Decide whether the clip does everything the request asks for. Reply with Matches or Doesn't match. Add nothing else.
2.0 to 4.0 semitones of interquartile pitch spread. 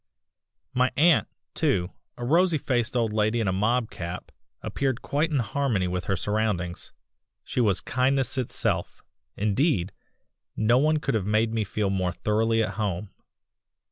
Doesn't match